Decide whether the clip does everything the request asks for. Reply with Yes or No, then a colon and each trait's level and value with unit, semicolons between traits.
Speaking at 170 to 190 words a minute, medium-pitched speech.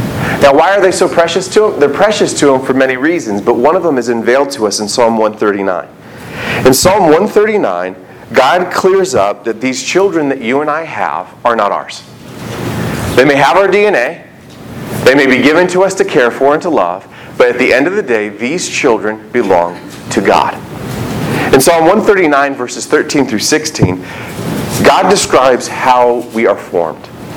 No: average, 185 wpm; low, 130 Hz